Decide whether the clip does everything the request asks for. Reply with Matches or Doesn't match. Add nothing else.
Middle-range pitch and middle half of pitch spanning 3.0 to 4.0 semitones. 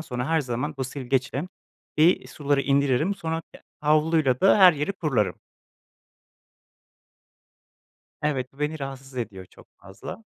Matches